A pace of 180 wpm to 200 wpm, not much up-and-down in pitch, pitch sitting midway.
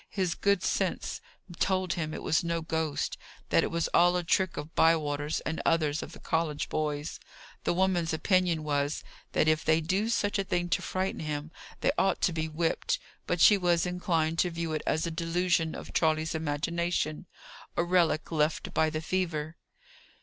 Yes: average, 185 wpm; narrow, 2.1 semitones; medium, 165 Hz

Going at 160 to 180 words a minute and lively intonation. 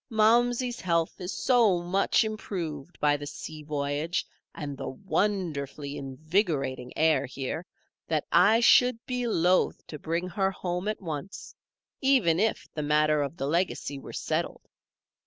No: average, 140 wpm; wide, 5.8 semitones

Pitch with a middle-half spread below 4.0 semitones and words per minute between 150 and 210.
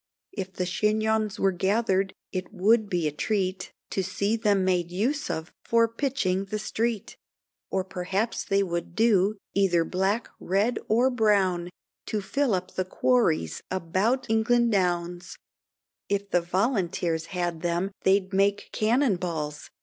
No: average, 3.4 semitones; average, 140 wpm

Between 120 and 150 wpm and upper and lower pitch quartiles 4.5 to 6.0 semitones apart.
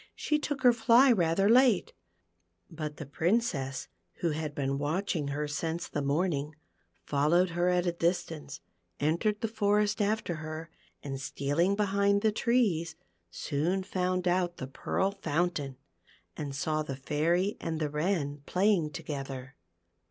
Yes: average, 140 wpm; average, 5.2 semitones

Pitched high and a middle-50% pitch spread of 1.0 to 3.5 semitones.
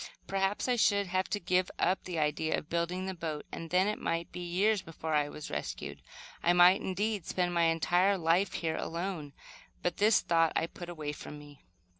No: medium, 175 Hz; average, 2.7 semitones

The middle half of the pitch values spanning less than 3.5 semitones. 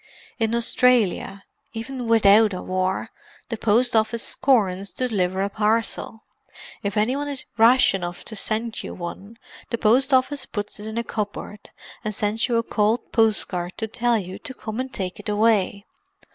Yes: average, 2.8 semitones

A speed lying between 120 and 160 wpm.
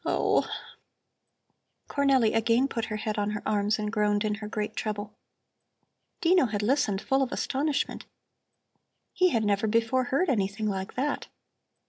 Yes: average, 145 wpm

